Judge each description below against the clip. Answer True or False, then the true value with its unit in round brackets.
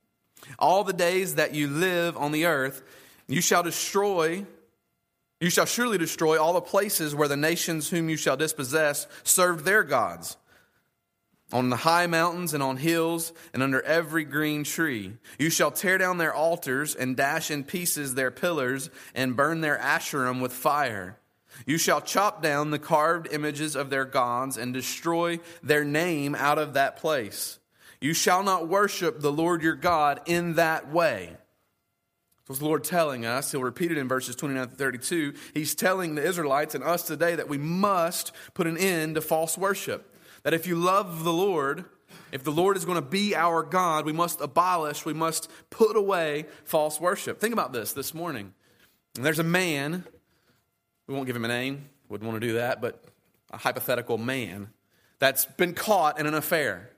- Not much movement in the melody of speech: False (3.8 semitones)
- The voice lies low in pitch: False (155 Hz)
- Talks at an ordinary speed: True (180 wpm)